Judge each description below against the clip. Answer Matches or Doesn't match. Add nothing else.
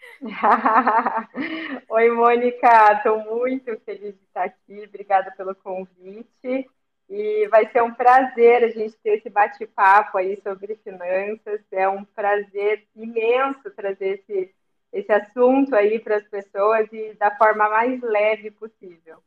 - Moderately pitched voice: Doesn't match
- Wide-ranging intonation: Doesn't match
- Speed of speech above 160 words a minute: Doesn't match